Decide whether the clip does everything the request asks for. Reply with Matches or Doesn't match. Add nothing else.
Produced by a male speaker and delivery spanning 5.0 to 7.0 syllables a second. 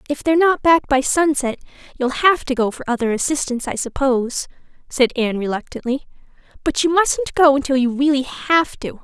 Doesn't match